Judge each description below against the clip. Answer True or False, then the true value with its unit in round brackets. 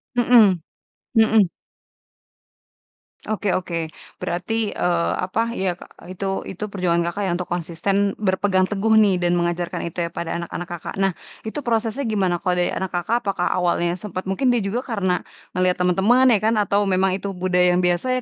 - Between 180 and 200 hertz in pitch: True (185 Hz)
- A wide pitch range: False (3.1 semitones)